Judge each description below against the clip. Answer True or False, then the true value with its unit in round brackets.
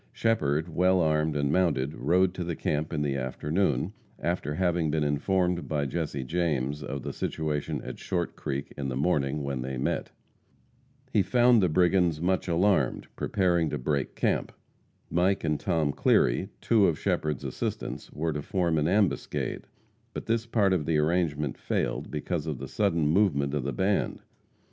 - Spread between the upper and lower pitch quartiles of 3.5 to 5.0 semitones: True (4.0 semitones)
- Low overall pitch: True (80 Hz)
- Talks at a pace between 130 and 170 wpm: True (165 wpm)